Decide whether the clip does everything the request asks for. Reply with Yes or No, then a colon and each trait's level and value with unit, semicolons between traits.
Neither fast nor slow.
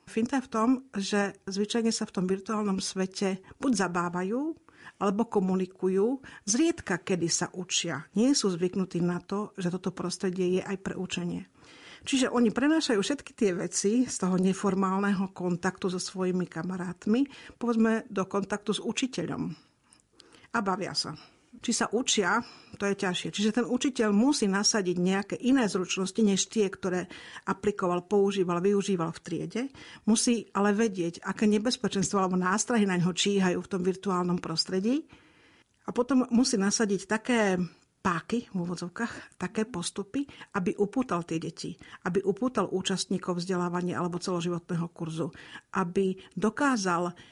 Yes: average, 140 wpm